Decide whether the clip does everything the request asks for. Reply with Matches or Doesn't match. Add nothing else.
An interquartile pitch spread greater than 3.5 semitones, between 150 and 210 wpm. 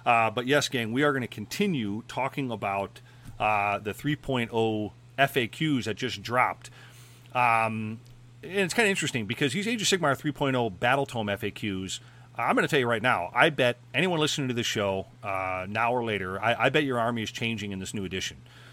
Matches